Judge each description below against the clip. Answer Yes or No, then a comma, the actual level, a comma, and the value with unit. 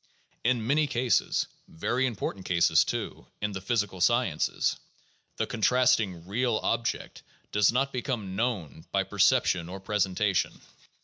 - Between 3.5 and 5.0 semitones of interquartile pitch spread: Yes, average, 4.6 semitones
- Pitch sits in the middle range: No, low, 105 Hz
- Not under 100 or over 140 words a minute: Yes, slow, 135 wpm